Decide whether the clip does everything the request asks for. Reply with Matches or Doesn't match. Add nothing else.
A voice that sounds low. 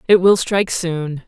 Doesn't match